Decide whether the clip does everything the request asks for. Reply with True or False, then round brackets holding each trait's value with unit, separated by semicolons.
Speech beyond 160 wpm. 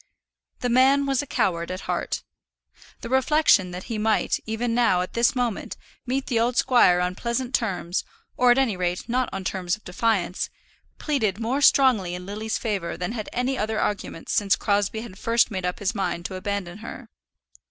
True (185 wpm)